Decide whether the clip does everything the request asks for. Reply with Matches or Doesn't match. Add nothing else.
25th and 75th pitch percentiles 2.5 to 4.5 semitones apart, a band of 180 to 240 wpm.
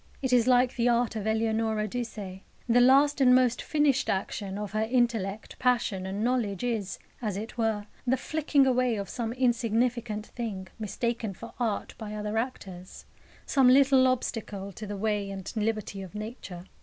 Doesn't match